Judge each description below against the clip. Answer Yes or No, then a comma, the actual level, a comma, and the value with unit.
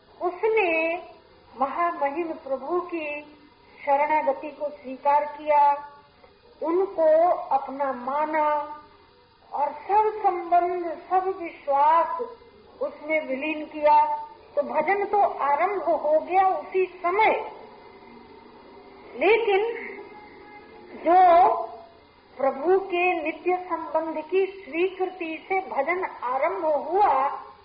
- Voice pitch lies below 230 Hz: No, very high, 345 Hz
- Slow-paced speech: Yes, slow, 90 wpm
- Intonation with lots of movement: No, average, 4.6 semitones